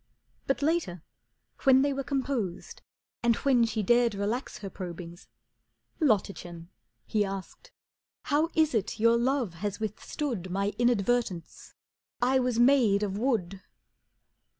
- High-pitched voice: Yes, high, 230 Hz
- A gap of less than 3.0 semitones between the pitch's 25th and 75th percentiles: No, average, 5.2 semitones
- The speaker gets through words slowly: Yes, slow, 125 wpm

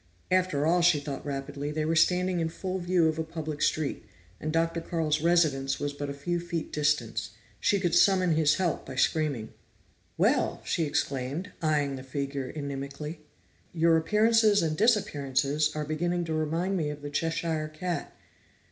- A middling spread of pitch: Yes, average, 3.1 semitones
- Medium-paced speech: Yes, average, 165 wpm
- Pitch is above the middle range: No, medium, 155 Hz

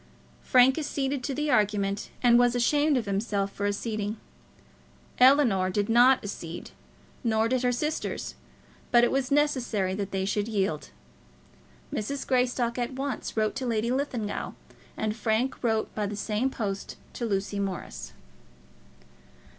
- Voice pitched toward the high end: Yes, high, 230 Hz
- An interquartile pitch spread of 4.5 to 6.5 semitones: No, average, 4.0 semitones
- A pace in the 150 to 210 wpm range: No, average, 140 wpm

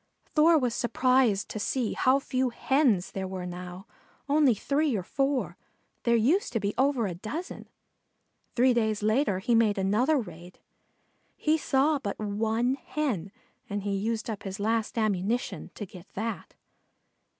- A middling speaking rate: Yes, average, 150 wpm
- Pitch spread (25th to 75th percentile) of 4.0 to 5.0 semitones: Yes, average, 4.7 semitones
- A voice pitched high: Yes, high, 230 Hz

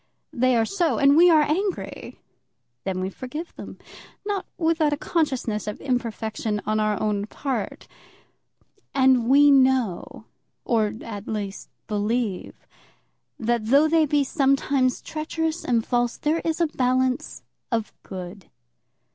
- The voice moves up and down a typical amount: No, wide, 5.7 semitones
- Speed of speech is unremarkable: No, slow, 130 wpm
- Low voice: No, very high, 255 Hz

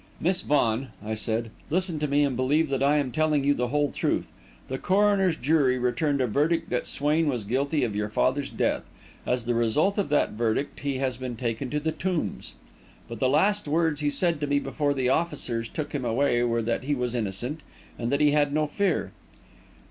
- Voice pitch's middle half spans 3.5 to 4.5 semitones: Yes, average, 3.8 semitones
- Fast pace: Yes, fast, 210 wpm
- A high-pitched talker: No, medium, 140 Hz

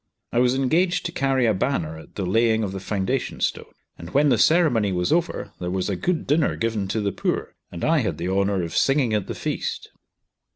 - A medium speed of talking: No, fast, 220 wpm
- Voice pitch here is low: Yes, low, 110 Hz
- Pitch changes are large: Yes, wide, 6.4 semitones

